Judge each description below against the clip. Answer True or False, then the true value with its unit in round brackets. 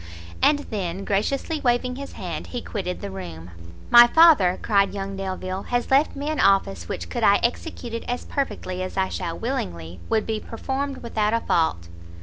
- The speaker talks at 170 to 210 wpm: True (180 wpm)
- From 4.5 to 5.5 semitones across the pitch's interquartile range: True (5.2 semitones)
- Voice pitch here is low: False (210 Hz)